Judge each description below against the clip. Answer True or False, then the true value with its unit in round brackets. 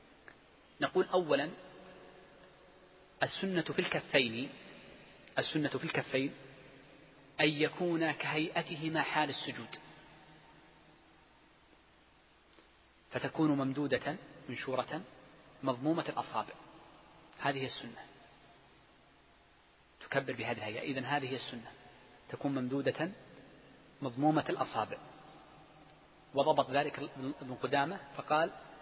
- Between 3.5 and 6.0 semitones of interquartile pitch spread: False (2.4 semitones)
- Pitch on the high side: False (145 Hz)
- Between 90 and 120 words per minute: False (75 wpm)